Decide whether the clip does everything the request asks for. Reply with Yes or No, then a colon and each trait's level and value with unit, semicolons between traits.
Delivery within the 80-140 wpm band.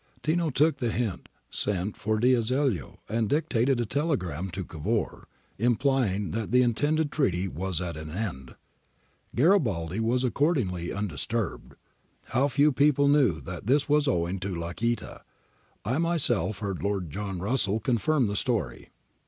Yes: slow, 135 wpm